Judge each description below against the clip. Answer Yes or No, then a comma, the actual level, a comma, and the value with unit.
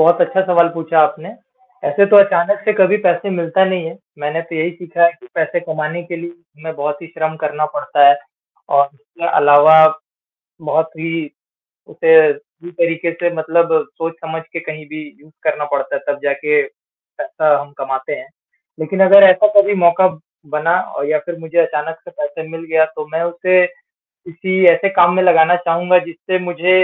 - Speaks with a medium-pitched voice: Yes, medium, 170 Hz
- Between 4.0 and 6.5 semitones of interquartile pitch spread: No, narrow, 2.5 semitones